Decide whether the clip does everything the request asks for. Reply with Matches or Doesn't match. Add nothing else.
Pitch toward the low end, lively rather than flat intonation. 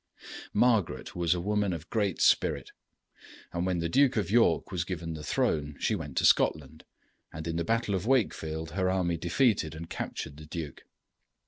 Doesn't match